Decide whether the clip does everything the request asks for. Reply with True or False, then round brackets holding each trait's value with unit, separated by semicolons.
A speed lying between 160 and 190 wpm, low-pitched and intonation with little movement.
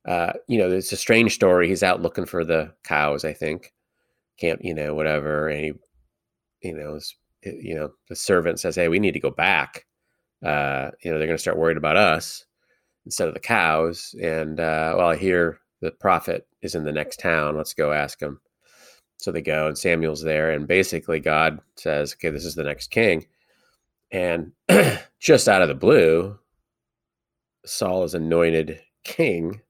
True (185 wpm; 80 Hz; 1.9 semitones)